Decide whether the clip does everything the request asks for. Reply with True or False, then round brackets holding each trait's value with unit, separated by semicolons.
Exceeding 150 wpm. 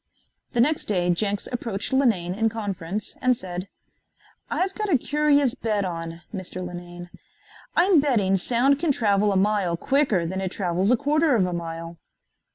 True (165 wpm)